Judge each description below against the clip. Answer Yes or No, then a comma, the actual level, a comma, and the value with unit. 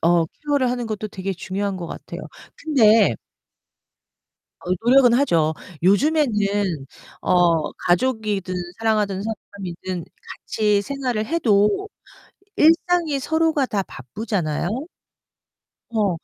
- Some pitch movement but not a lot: No, wide, 5.7 semitones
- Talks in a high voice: Yes, high, 210 Hz